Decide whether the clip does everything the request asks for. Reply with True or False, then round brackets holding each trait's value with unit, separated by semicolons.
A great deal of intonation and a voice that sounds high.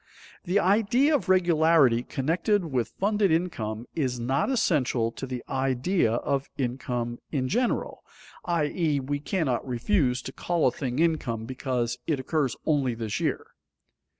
False (5.8 semitones; 140 Hz)